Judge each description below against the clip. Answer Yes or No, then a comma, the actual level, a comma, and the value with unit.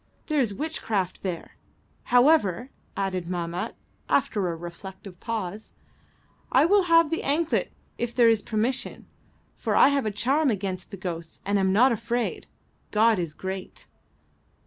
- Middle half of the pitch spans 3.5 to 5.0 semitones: No, wide, 5.6 semitones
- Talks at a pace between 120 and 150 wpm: Yes, average, 145 wpm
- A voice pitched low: No, high, 210 Hz